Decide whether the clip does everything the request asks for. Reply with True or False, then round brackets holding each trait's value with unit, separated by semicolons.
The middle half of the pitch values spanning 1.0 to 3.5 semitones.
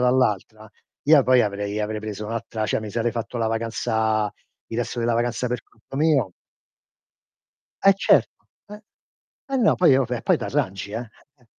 True (2.6 semitones)